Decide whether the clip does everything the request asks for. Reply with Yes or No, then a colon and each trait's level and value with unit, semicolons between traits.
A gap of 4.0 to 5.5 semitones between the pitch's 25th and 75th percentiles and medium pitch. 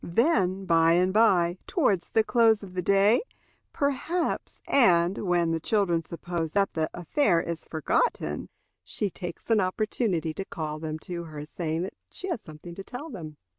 Yes: average, 4.6 semitones; medium, 180 Hz